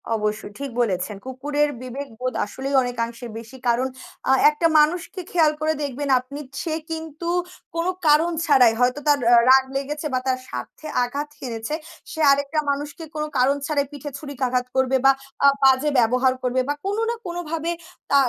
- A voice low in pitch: No, very high, 275 Hz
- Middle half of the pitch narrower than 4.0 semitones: Yes, average, 3.2 semitones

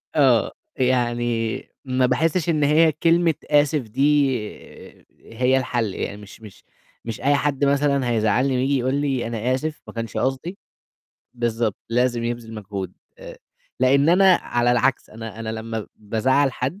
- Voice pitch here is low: Yes, low, 130 Hz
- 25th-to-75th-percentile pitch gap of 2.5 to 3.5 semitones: No, average, 3.9 semitones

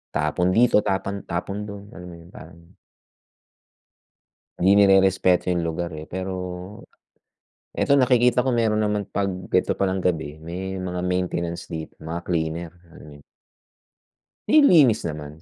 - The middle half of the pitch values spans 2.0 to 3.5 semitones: Yes, average, 3.1 semitones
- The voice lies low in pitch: Yes, very low, 90 Hz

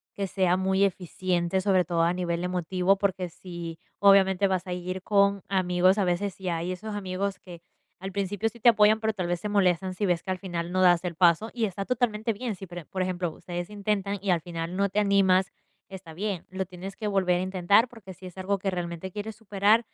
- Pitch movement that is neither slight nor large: No, narrow, 2.1 semitones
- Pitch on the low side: No, high, 190 Hz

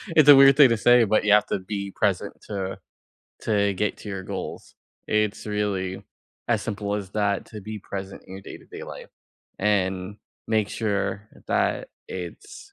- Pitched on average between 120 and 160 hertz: No, low, 105 Hz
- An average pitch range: No, narrow, 1.9 semitones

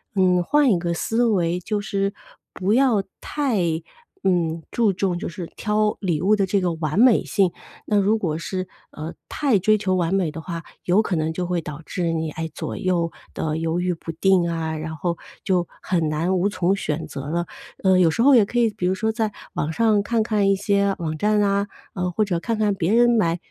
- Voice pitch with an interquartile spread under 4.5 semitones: Yes, average, 3.8 semitones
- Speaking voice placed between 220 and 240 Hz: No, medium, 185 Hz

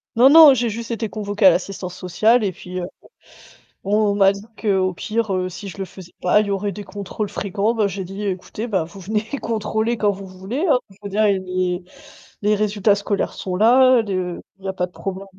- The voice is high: Yes, high, 200 Hz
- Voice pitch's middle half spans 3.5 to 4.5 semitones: No, narrow, 2.5 semitones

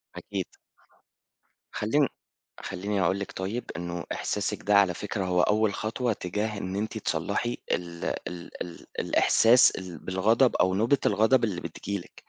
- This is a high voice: No, low, 100 Hz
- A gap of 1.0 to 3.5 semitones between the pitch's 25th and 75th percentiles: Yes, average, 3.2 semitones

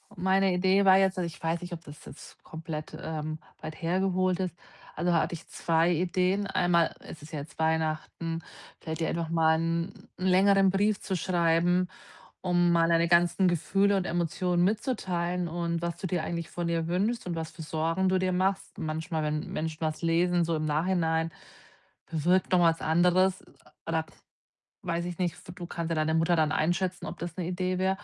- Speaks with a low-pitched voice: No, medium, 170 Hz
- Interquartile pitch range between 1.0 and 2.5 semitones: Yes, narrow, 2.2 semitones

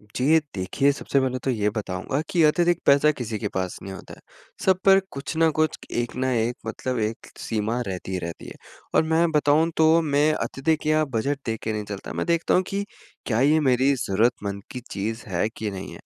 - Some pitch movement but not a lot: No, wide, 6.3 semitones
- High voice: No, low, 130 Hz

